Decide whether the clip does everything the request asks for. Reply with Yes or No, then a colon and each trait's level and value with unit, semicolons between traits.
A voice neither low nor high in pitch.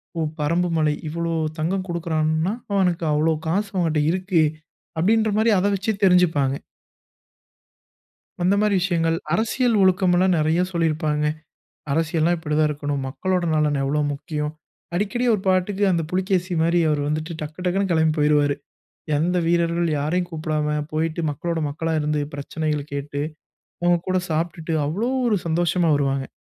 Yes: medium, 165 Hz